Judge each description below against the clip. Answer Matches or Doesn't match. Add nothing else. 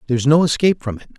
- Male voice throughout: Matches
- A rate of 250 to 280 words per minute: Matches